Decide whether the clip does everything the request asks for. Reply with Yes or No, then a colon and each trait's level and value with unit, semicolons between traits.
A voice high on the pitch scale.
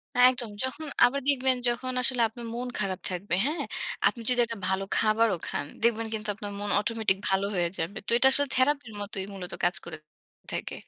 Yes: high, 225 Hz